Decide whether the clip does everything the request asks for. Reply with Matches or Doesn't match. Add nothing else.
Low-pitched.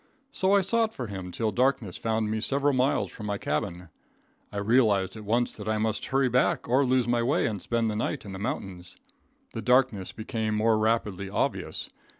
Matches